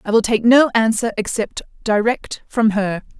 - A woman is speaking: Yes, female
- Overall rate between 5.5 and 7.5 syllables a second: No, 4.5 syllables/s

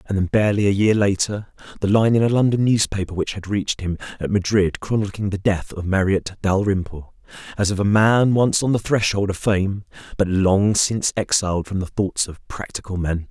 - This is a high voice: No, low, 100 Hz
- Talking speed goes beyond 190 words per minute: Yes, average, 200 wpm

